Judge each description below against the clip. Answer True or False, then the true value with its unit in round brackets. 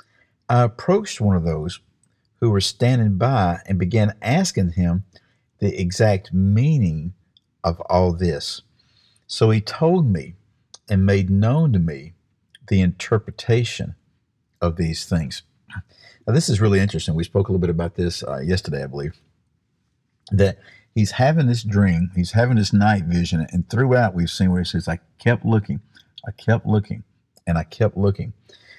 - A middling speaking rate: True (160 wpm)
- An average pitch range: True (4.5 semitones)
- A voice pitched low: True (100 Hz)